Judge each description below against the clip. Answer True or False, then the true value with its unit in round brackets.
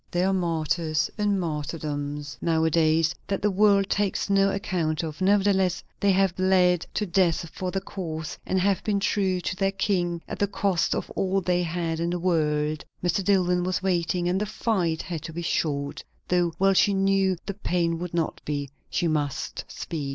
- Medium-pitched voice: True (180 Hz)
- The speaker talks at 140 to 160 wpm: False (190 wpm)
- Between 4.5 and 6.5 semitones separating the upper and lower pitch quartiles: False (3.1 semitones)